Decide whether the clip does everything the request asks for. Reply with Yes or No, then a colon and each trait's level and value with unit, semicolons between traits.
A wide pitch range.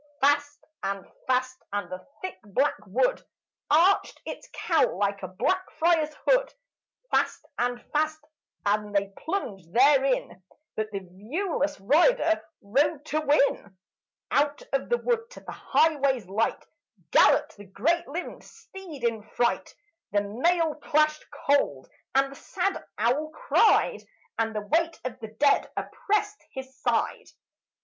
Yes: wide, 7.2 semitones